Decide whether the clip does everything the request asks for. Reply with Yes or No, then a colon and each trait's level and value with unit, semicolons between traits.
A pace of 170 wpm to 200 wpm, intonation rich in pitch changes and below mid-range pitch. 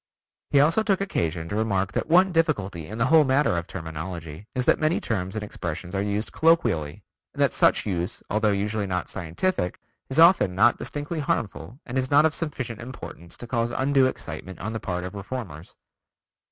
Yes: average, 190 wpm; wide, 7.6 semitones; low, 110 Hz